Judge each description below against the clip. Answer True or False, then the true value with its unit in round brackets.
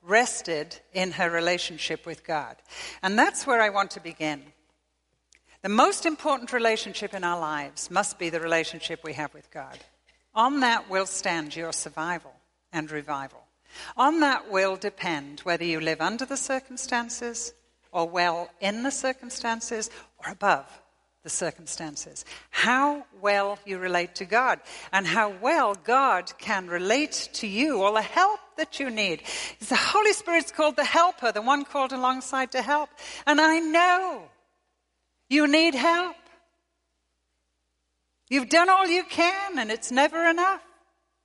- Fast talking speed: False (150 wpm)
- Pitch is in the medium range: False (225 Hz)